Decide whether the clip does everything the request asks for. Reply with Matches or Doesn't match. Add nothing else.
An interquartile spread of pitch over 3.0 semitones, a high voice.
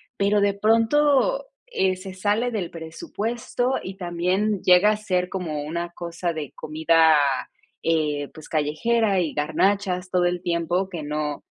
Doesn't match